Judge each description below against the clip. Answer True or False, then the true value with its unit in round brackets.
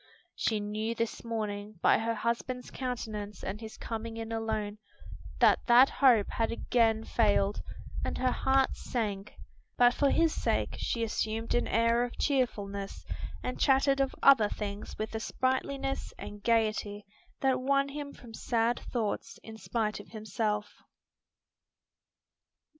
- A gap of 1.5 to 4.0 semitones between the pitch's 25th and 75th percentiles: True (2.8 semitones)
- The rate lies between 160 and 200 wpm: False (140 wpm)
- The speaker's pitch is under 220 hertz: False (225 Hz)